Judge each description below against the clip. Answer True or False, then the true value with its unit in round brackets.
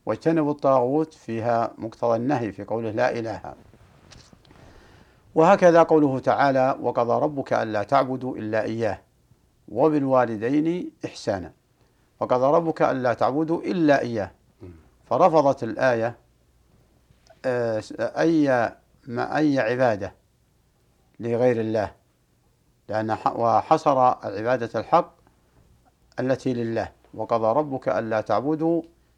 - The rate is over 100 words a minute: False (90 wpm)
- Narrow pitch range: False (4.5 semitones)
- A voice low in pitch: True (120 Hz)